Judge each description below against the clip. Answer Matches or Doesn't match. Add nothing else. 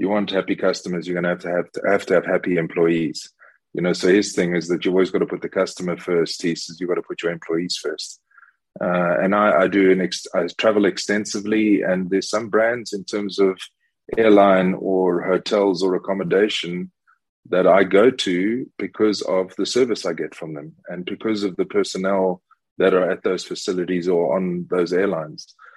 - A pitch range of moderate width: Doesn't match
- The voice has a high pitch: Doesn't match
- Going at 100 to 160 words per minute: Doesn't match